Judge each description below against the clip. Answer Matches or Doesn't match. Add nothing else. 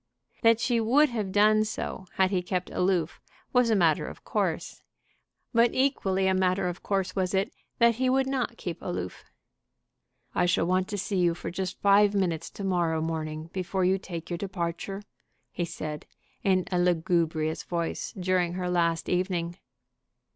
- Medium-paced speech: Matches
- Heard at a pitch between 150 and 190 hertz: Matches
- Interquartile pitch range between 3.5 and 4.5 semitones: Doesn't match